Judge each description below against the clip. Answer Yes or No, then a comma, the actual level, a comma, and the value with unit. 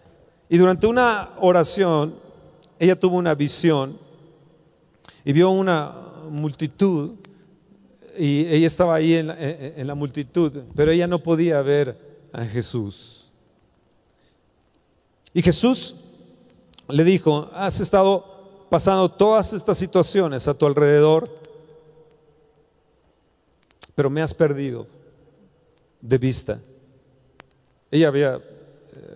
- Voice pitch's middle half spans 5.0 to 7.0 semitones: No, average, 3.7 semitones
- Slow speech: Yes, slow, 100 wpm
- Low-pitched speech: No, medium, 160 Hz